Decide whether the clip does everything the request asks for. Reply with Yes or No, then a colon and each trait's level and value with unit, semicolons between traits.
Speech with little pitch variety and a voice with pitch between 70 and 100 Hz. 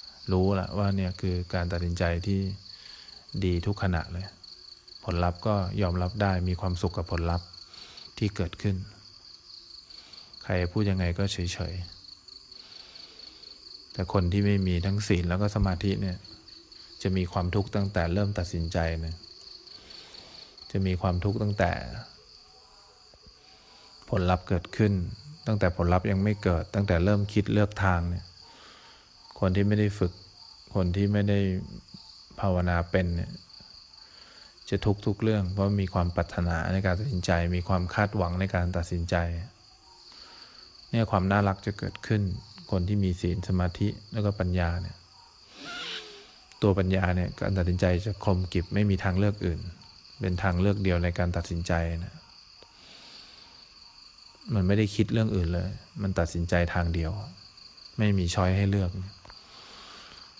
Yes: narrow, 2.3 semitones; very low, 95 Hz